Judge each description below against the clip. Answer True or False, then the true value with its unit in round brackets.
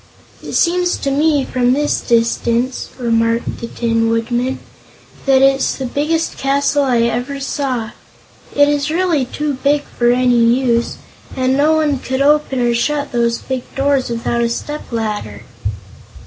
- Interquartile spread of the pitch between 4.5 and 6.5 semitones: False (3.4 semitones)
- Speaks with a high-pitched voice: True (260 Hz)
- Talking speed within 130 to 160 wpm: True (150 wpm)